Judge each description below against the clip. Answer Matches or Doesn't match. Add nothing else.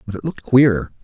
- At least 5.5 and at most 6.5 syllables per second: Matches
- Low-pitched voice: Matches